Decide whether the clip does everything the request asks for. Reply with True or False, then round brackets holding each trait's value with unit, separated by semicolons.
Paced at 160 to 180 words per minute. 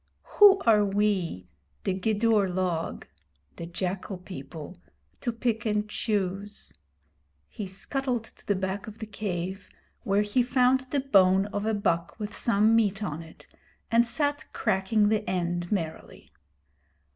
False (140 wpm)